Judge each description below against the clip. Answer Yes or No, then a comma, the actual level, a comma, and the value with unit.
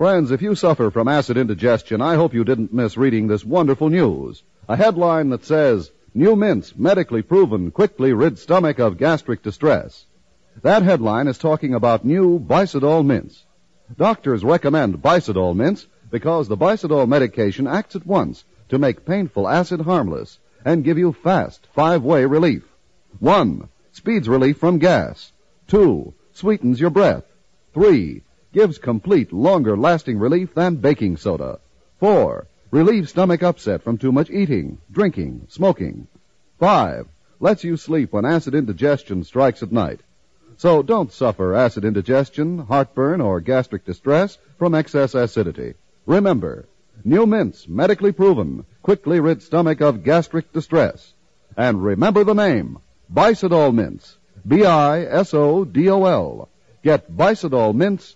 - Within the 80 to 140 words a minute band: Yes, slow, 135 wpm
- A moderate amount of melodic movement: No, wide, 6.6 semitones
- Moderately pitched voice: Yes, medium, 155 Hz